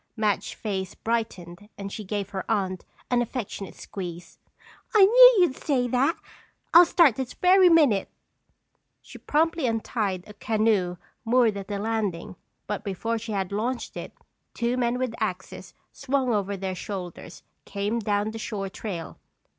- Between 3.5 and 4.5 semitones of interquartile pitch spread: Yes, average, 4.1 semitones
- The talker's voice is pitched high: Yes, high, 215 Hz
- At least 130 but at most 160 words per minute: Yes, average, 150 wpm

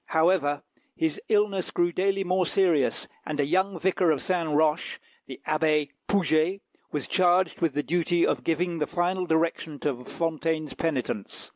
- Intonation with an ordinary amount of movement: Yes, average, 3.0 semitones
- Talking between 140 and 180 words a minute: Yes, average, 155 wpm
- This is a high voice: No, medium, 165 Hz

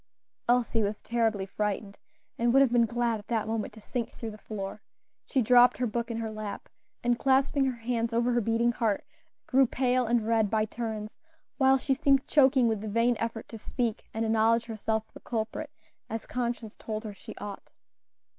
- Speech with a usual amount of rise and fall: No, narrow, 2.0 semitones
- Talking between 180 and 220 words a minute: Yes, average, 195 wpm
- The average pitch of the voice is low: No, high, 230 Hz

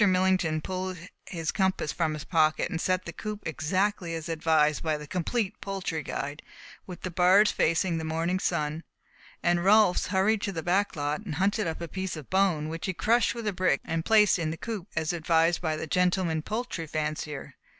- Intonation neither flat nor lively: Yes, average, 3.2 semitones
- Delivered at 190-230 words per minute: Yes, average, 195 wpm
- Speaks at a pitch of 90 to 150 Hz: No, medium, 175 Hz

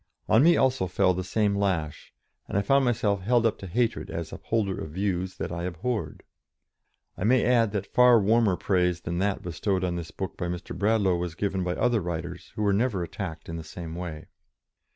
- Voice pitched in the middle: No, very low, 95 Hz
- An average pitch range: Yes, average, 4.0 semitones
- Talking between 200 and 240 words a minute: Yes, fast, 205 wpm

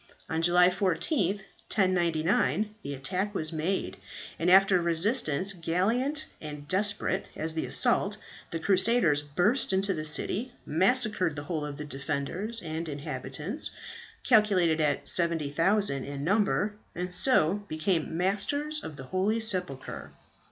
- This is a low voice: No, medium, 180 Hz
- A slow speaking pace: Yes, slow, 130 wpm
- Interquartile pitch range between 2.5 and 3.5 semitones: No, average, 4.7 semitones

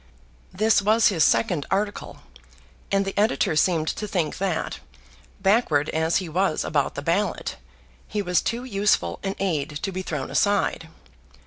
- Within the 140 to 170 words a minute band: Yes, average, 150 wpm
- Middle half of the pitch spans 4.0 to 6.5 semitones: Yes, average, 4.3 semitones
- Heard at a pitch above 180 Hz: Yes, high, 190 Hz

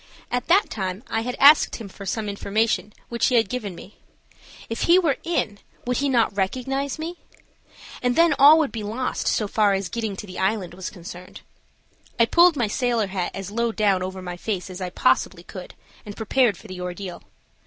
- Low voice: No, high, 215 Hz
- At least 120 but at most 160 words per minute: No, average, 200 wpm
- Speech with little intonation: No, average, 4.7 semitones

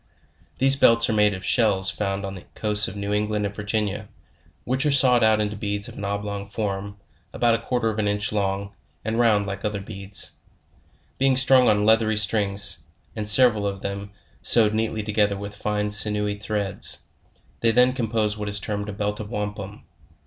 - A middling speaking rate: Yes, average, 185 wpm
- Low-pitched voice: Yes, low, 105 Hz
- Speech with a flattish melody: Yes, narrow, 1.4 semitones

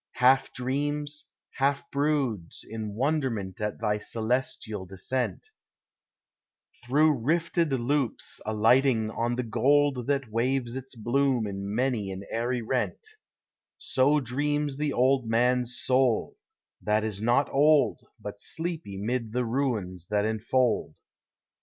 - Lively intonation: No, average, 4.0 semitones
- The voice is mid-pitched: No, low, 125 Hz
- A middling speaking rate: No, slow, 120 wpm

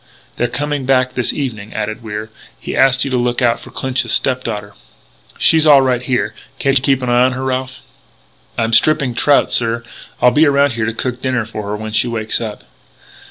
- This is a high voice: No, low, 125 Hz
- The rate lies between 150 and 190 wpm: No, fast, 205 wpm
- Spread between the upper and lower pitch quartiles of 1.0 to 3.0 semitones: Yes, average, 2.7 semitones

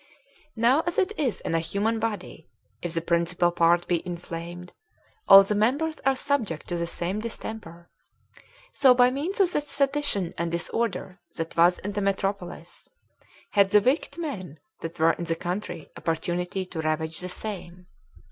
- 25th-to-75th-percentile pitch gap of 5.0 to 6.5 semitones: Yes, wide, 5.4 semitones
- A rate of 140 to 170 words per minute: Yes, average, 165 wpm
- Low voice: No, medium, 185 Hz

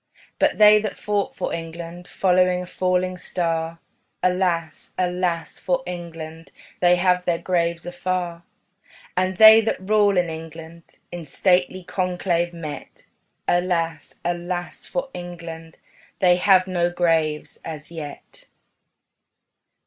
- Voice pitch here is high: No, medium, 175 Hz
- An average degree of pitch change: No, narrow, 1.7 semitones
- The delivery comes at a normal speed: No, slow, 120 wpm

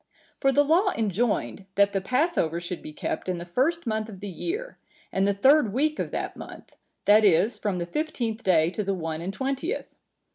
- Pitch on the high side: Yes, high, 215 Hz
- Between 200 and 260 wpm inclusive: Yes, fast, 205 wpm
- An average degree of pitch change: No, wide, 6.8 semitones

